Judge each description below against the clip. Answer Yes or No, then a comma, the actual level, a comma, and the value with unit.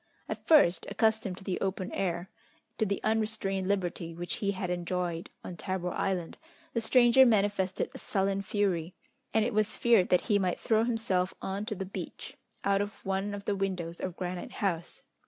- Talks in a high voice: Yes, high, 195 Hz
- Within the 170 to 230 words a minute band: Yes, average, 180 wpm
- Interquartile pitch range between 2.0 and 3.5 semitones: Yes, average, 2.7 semitones